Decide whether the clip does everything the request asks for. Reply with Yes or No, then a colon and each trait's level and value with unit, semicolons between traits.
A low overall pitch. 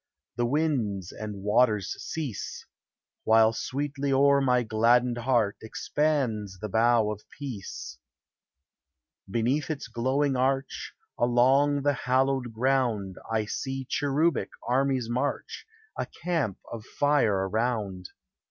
Yes: low, 125 Hz